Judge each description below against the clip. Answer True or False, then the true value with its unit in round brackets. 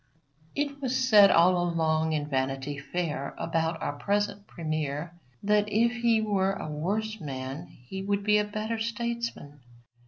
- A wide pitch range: True (5.8 semitones)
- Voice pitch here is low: False (190 Hz)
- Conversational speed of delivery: True (150 wpm)